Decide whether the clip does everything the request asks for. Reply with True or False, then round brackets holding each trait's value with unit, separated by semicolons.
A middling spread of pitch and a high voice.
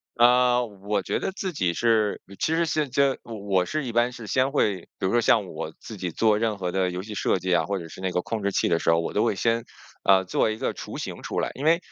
False (4.6 semitones; 105 Hz)